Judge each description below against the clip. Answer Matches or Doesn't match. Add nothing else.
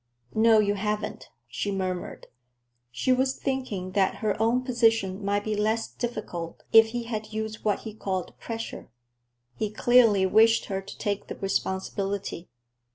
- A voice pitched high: Matches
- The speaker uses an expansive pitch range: Doesn't match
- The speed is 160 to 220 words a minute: Doesn't match